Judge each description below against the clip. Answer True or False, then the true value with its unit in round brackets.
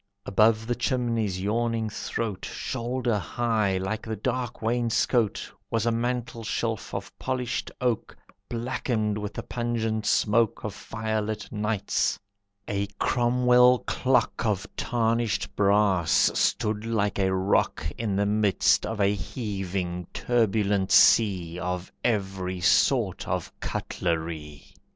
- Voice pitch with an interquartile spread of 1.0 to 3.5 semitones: True (2.9 semitones)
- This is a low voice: True (110 Hz)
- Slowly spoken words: True (115 wpm)